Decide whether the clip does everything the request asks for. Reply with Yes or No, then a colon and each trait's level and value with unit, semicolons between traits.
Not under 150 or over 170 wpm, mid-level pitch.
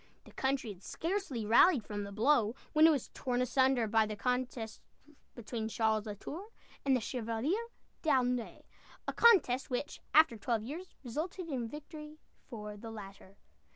No: average, 155 wpm; high, 245 Hz